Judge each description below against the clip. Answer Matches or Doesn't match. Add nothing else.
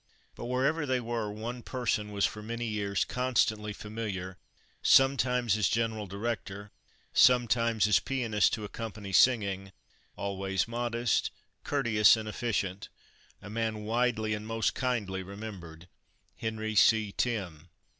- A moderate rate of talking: Doesn't match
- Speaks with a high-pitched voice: Doesn't match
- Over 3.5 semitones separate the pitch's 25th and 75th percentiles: Doesn't match